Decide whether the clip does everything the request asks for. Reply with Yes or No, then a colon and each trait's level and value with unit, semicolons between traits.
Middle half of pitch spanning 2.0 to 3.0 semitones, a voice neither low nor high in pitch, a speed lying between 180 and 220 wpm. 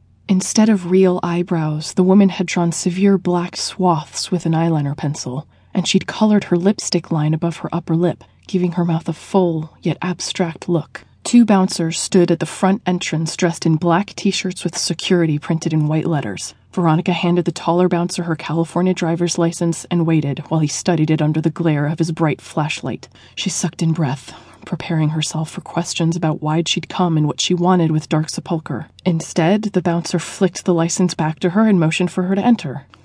Yes: narrow, 2.4 semitones; medium, 170 Hz; average, 195 wpm